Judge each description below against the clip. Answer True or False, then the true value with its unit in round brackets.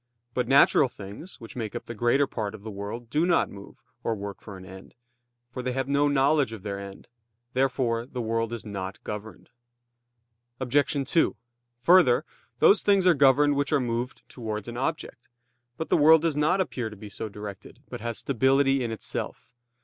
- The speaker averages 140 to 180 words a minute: False (190 wpm)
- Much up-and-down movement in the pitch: False (4.8 semitones)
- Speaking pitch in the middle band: False (120 Hz)